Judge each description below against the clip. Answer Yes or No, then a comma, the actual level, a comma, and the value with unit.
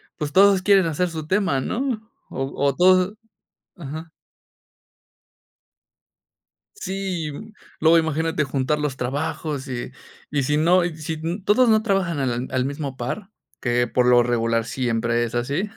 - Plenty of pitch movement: Yes, wide, 6.0 semitones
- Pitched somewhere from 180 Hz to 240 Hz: No, medium, 155 Hz